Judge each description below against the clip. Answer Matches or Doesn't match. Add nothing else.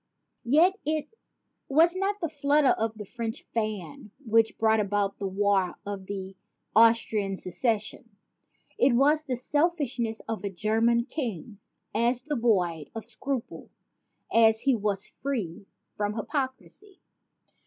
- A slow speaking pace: Matches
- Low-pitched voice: Doesn't match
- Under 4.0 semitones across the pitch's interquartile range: Doesn't match